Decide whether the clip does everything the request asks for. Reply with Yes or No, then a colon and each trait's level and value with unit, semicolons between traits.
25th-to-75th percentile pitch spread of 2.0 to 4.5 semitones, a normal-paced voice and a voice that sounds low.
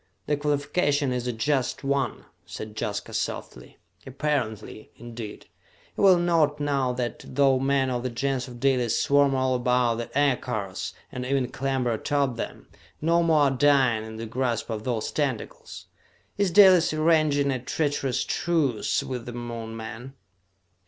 Yes: average, 3.3 semitones; average, 150 wpm; low, 130 Hz